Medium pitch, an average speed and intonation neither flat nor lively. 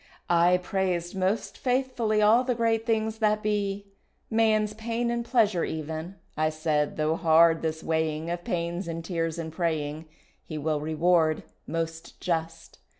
Yes: medium, 175 Hz; average, 150 wpm; average, 5.0 semitones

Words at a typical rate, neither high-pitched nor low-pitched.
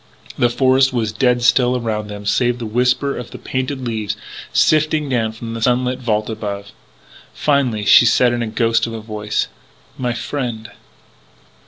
No: average, 165 wpm; low, 120 Hz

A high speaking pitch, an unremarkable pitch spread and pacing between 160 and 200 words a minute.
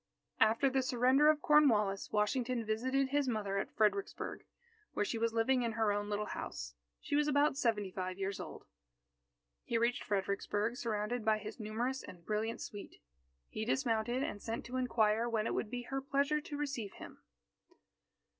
Yes: high, 230 Hz; average, 3.8 semitones; average, 170 wpm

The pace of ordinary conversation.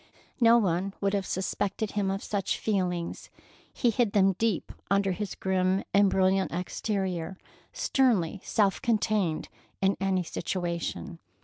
No: slow, 130 wpm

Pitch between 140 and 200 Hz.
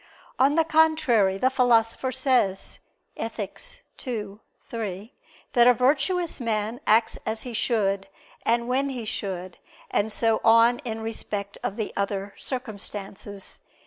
No: high, 225 Hz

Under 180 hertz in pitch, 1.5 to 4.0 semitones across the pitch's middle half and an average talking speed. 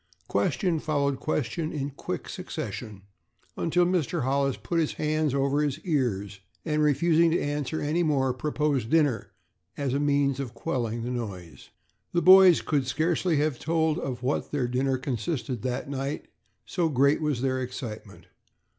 Yes: medium, 140 Hz; average, 3.5 semitones; average, 155 wpm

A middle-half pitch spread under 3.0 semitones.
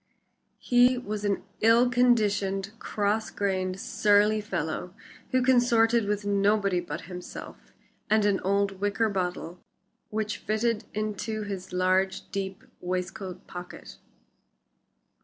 Yes: narrow, 2.4 semitones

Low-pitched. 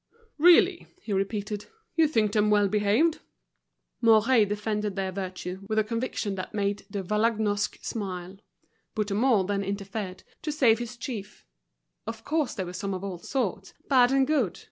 No: high, 210 Hz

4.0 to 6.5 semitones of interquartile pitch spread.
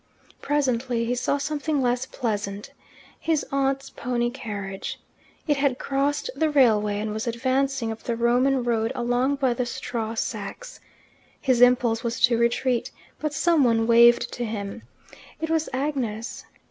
No: average, 3.0 semitones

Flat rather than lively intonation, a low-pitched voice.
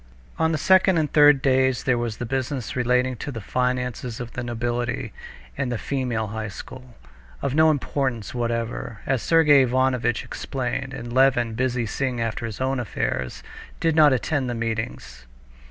Yes: narrow, 2.3 semitones; low, 125 Hz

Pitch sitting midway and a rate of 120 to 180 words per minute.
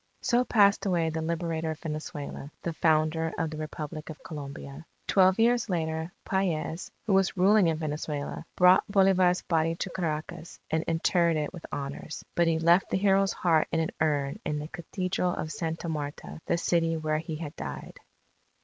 Yes: medium, 165 Hz; average, 175 wpm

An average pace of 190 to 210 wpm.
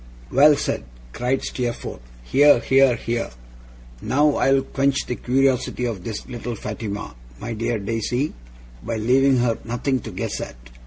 No: average, 145 wpm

